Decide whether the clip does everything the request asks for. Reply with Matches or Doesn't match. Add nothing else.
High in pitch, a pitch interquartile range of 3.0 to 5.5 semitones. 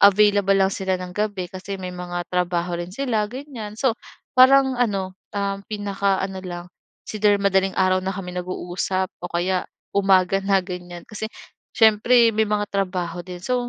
Doesn't match